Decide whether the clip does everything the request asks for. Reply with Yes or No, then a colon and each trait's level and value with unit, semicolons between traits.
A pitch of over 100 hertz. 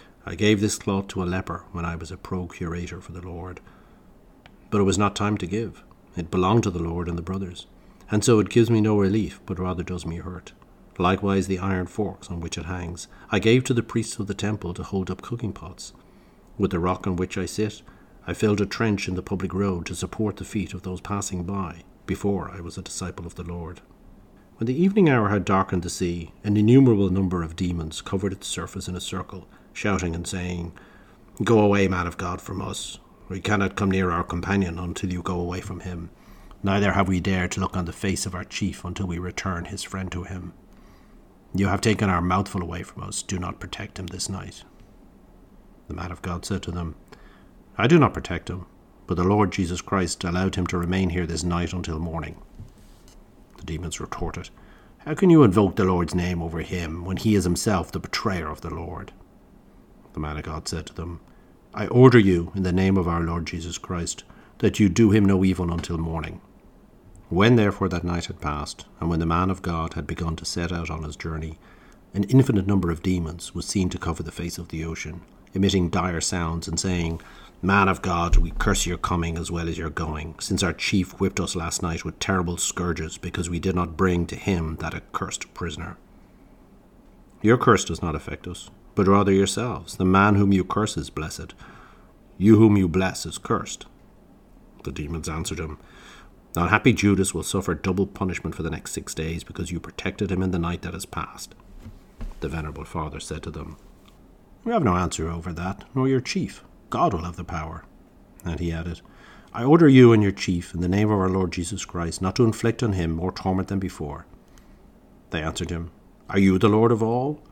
No: very low, 90 Hz